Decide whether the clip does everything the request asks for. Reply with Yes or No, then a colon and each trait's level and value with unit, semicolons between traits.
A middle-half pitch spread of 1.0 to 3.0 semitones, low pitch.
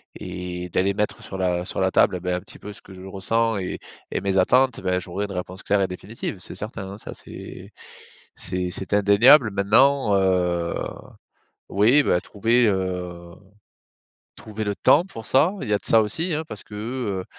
No: average, 3.5 semitones; low, 100 Hz